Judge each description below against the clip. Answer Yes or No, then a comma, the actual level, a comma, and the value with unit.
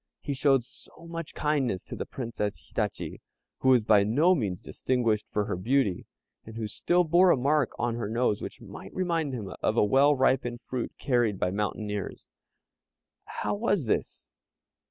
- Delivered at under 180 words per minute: Yes, average, 170 wpm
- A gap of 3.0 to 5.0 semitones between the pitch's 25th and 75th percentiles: No, wide, 5.5 semitones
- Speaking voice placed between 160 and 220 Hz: No, low, 125 Hz